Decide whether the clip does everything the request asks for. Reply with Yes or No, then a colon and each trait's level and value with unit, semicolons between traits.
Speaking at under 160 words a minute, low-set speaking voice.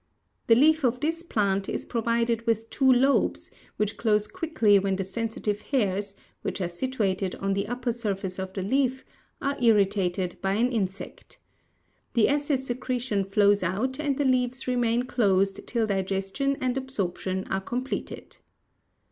No: average, 150 wpm; high, 225 Hz